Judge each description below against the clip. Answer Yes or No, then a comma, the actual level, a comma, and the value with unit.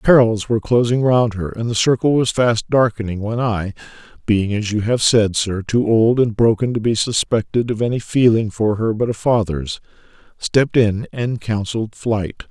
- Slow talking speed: No, average, 180 wpm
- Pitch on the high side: No, low, 110 Hz